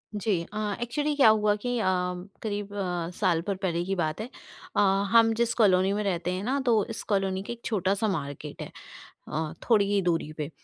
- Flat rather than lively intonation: No, average, 3.8 semitones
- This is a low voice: No, high, 200 Hz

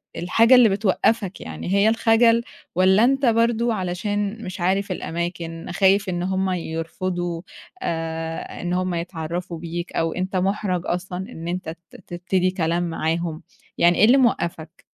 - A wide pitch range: No, average, 3.1 semitones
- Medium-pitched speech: Yes, medium, 180 Hz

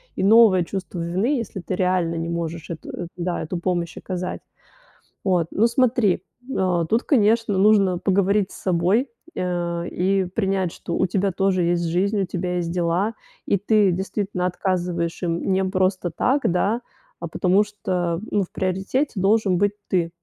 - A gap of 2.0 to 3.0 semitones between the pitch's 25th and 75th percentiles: Yes, narrow, 2.5 semitones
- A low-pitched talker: No, medium, 185 Hz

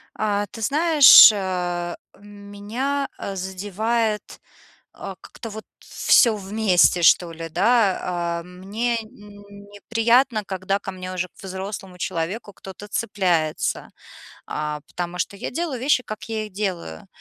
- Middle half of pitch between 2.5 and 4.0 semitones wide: Yes, average, 3.2 semitones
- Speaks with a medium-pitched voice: No, high, 200 Hz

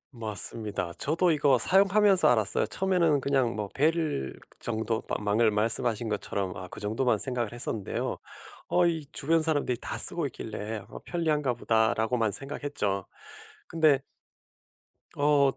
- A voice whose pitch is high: No, low, 125 Hz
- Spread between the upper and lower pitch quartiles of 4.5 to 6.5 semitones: Yes, wide, 5.9 semitones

